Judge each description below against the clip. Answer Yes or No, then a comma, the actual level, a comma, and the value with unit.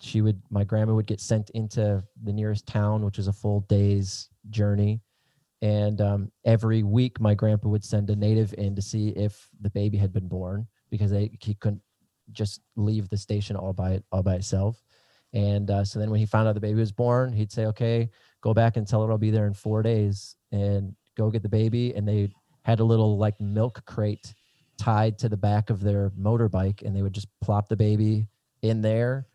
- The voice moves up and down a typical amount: No, narrow, 1.5 semitones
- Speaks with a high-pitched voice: No, low, 105 Hz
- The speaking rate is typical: No, fast, 215 wpm